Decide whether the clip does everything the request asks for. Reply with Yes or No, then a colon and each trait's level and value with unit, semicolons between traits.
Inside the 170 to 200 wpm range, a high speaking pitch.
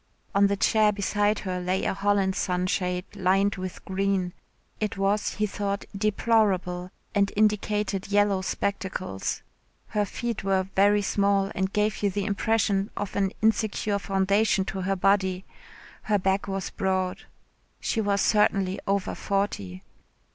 No: average, 140 wpm; high, 195 Hz